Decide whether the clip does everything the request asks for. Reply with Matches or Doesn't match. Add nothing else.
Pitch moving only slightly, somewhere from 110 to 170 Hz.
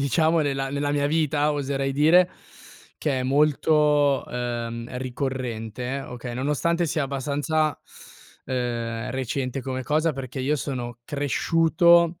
Doesn't match